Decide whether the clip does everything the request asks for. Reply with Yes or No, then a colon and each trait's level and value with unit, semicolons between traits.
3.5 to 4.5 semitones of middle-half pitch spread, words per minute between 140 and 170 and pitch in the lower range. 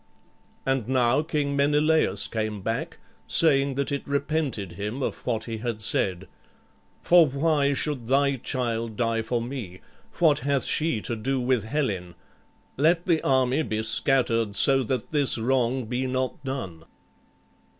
Yes: average, 3.9 semitones; average, 145 wpm; low, 130 Hz